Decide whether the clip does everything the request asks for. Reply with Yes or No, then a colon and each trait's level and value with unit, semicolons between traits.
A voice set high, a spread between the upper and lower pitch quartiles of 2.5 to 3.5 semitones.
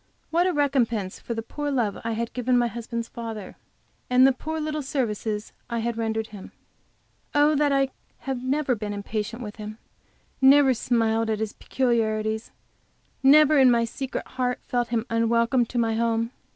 Yes: high, 235 Hz; average, 3.1 semitones